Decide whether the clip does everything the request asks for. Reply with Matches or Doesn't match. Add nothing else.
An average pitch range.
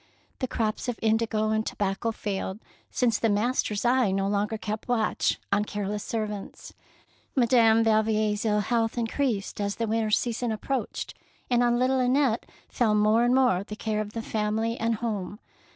Doesn't match